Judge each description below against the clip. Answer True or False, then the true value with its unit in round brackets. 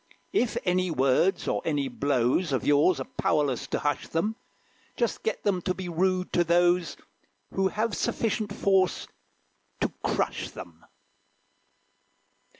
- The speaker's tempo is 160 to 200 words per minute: False (135 wpm)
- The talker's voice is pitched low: False (175 Hz)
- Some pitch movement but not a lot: True (4.8 semitones)